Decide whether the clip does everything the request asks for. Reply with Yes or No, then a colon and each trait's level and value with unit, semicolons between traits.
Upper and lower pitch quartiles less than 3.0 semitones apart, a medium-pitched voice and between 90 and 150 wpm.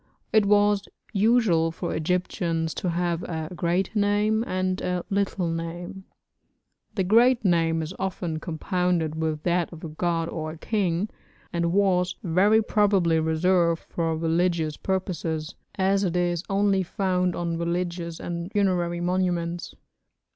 Yes: narrow, 2.5 semitones; medium, 175 Hz; slow, 135 wpm